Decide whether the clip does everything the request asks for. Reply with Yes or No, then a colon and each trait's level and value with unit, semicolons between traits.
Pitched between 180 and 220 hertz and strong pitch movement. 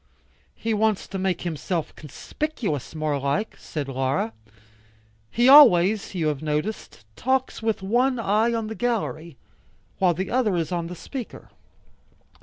Yes: high, 190 Hz; wide, 6.6 semitones